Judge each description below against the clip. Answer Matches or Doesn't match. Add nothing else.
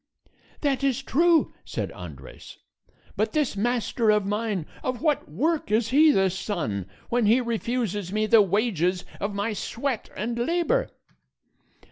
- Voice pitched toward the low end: Doesn't match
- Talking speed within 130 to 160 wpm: Matches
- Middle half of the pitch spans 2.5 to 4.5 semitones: Doesn't match